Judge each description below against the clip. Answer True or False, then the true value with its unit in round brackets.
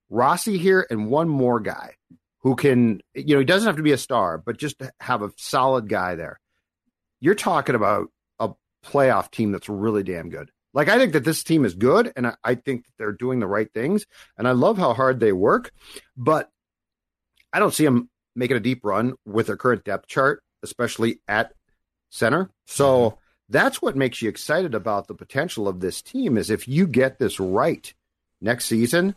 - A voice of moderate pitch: False (125 Hz)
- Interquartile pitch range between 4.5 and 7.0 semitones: True (5.1 semitones)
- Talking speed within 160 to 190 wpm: False (200 wpm)